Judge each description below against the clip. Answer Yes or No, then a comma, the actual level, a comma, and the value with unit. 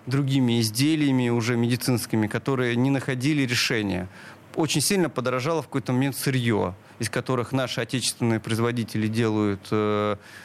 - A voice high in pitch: No, low, 125 Hz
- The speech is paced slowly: No, average, 125 wpm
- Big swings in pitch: No, average, 3.3 semitones